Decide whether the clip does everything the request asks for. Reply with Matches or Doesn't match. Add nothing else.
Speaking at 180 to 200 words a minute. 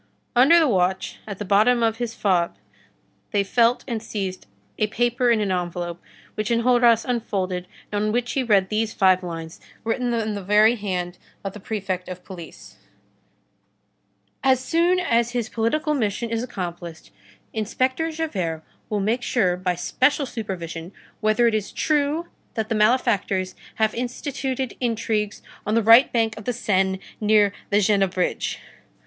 Doesn't match